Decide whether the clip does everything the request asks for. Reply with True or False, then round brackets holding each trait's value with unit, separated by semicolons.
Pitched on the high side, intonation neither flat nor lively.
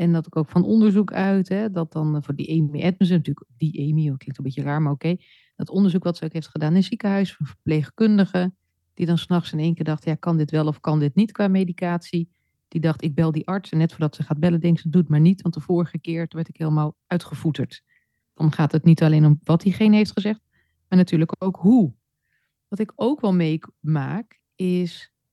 False (165 Hz; 3.2 semitones)